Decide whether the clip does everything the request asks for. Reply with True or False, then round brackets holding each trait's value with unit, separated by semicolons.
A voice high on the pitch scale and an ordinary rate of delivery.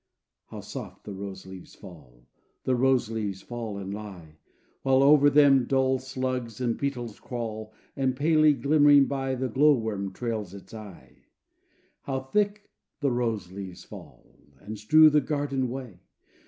False (125 Hz; 150 wpm)